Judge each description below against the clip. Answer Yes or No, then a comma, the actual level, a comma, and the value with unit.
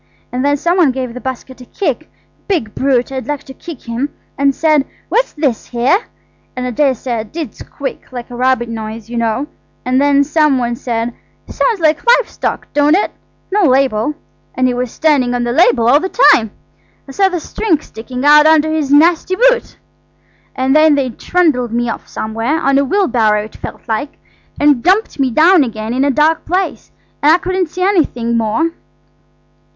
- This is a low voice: No, very high, 275 Hz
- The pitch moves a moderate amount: Yes, average, 4.6 semitones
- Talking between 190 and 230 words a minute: No, average, 180 wpm